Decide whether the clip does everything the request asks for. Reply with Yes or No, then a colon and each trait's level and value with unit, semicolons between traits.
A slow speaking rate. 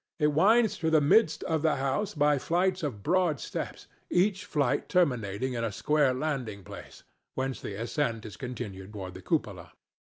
No: average, 170 wpm